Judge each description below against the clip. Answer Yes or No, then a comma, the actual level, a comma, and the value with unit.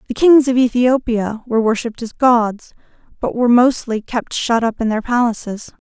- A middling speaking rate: Yes, average, 175 wpm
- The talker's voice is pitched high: Yes, high, 235 Hz